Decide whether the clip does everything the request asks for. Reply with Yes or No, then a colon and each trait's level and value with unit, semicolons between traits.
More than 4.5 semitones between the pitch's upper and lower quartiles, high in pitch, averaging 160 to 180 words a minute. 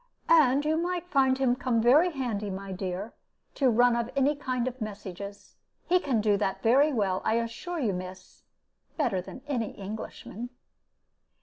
Yes: average, 5.3 semitones; high, 240 Hz; average, 165 wpm